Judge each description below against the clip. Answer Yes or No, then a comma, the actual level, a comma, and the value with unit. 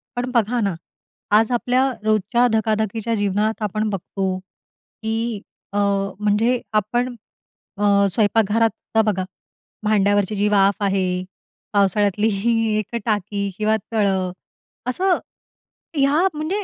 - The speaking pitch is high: Yes, high, 215 Hz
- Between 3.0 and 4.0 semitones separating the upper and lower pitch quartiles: No, narrow, 2.5 semitones